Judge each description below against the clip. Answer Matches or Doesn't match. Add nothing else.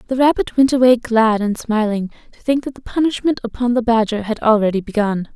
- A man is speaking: Doesn't match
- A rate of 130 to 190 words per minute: Doesn't match